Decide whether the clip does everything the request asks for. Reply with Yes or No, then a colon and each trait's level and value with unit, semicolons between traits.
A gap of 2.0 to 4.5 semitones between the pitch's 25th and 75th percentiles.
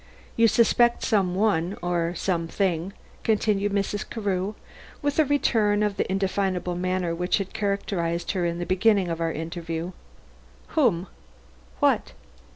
Yes: average, 3.1 semitones